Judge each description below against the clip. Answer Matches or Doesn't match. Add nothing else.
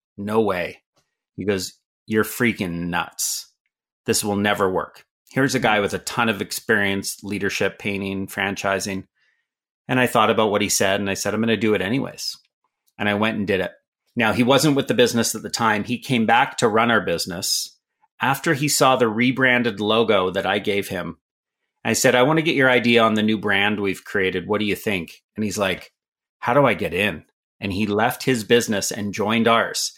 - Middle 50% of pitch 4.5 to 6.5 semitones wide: Doesn't match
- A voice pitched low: Matches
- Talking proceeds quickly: Matches